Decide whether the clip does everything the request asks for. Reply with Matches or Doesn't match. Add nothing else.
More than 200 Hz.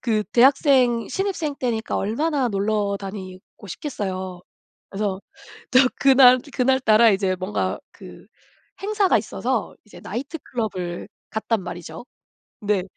Matches